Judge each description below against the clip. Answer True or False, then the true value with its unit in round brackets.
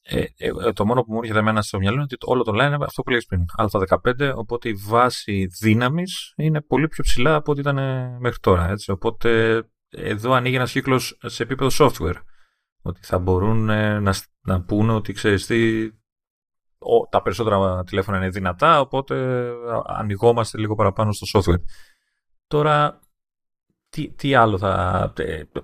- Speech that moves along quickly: False (155 wpm)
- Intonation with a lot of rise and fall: False (4.4 semitones)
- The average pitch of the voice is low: True (115 Hz)